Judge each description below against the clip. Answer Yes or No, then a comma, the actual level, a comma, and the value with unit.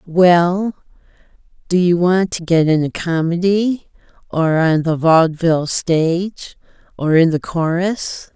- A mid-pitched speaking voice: Yes, medium, 170 Hz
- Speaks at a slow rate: Yes, slow, 130 wpm